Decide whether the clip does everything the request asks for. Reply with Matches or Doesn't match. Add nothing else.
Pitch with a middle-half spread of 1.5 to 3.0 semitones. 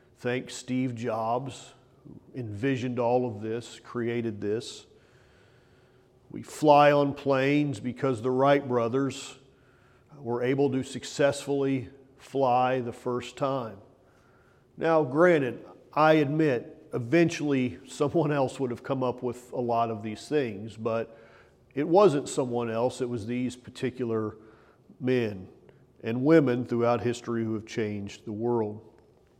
Matches